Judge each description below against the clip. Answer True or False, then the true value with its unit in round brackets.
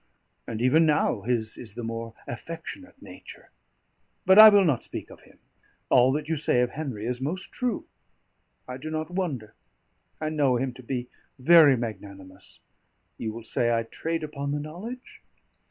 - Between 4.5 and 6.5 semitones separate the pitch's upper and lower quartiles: True (5.3 semitones)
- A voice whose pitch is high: False (135 Hz)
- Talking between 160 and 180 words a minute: True (170 wpm)